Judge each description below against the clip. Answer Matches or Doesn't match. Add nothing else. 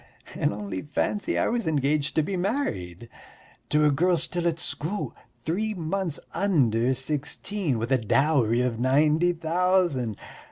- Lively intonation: Matches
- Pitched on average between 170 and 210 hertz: Doesn't match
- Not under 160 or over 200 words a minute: Doesn't match